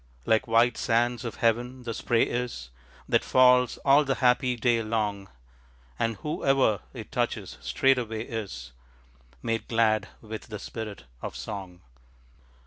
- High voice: No, low, 115 Hz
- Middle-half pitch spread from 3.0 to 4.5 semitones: No, narrow, 2.4 semitones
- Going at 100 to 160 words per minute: Yes, slow, 135 wpm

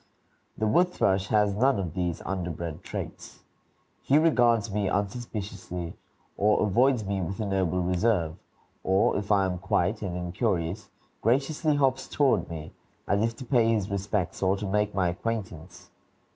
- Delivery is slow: No, average, 155 wpm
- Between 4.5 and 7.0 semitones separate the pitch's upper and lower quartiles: No, average, 3.9 semitones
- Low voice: Yes, low, 100 Hz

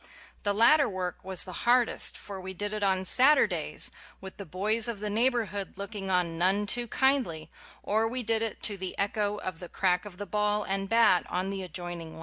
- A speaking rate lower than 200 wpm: No, fast, 205 wpm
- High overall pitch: Yes, high, 200 Hz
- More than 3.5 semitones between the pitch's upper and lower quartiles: No, average, 3.0 semitones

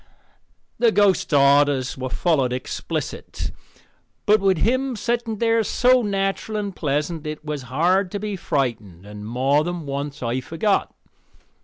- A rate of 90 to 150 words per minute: Yes, average, 140 wpm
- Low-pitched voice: No, medium, 160 Hz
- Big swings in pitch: Yes, wide, 7.1 semitones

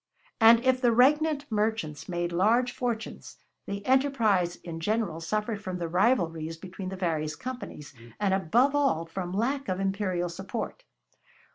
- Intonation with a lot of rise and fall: Yes, wide, 5.7 semitones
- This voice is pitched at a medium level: No, high, 200 Hz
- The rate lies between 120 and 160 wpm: Yes, average, 145 wpm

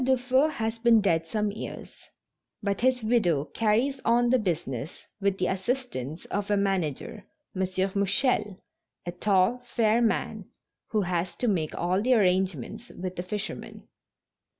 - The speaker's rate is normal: Yes, average, 145 wpm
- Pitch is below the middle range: No, high, 205 Hz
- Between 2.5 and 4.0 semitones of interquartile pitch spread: No, average, 4.6 semitones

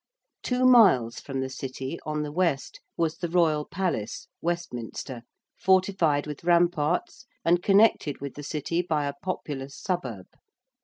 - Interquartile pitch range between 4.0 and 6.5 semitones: Yes, average, 4.5 semitones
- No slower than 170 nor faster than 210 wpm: No, average, 140 wpm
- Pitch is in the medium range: Yes, medium, 160 Hz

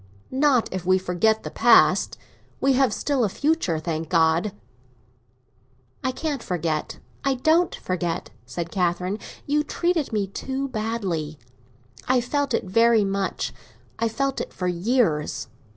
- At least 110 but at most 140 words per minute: Yes, slow, 135 wpm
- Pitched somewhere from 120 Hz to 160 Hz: No, high, 220 Hz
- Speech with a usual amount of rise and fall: No, wide, 6.9 semitones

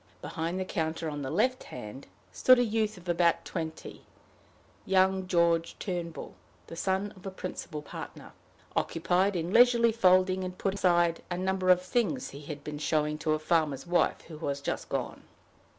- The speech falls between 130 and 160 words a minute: No, average, 170 wpm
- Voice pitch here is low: No, medium, 175 Hz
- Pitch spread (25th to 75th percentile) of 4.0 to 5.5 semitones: No, average, 3.1 semitones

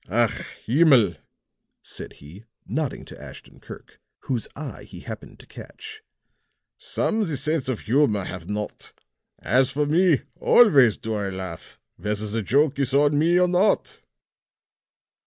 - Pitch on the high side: No, low, 135 Hz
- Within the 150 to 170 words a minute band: No, average, 140 wpm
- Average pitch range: No, wide, 6.5 semitones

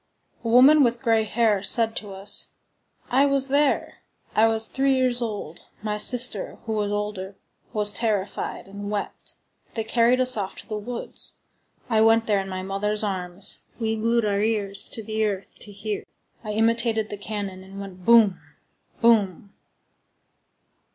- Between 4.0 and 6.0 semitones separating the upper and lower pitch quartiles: No, narrow, 2.5 semitones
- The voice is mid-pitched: No, high, 215 Hz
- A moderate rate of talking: Yes, average, 160 wpm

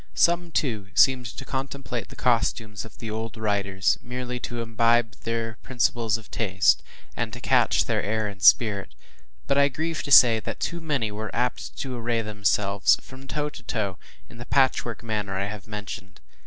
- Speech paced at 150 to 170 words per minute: No, average, 180 wpm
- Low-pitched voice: Yes, low, 115 Hz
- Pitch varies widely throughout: No, average, 3.4 semitones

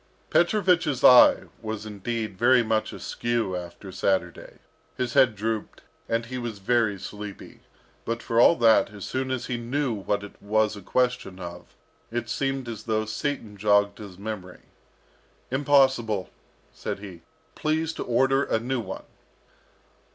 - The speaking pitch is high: No, low, 115 Hz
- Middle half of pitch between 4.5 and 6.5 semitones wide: No, average, 3.8 semitones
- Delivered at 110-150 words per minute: Yes, average, 145 wpm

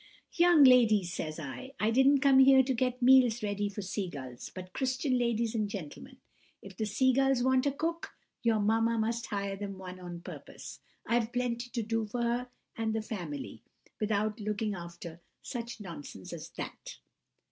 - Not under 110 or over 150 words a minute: No, average, 175 wpm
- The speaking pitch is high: Yes, high, 225 Hz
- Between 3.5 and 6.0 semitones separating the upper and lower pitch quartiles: Yes, average, 4.1 semitones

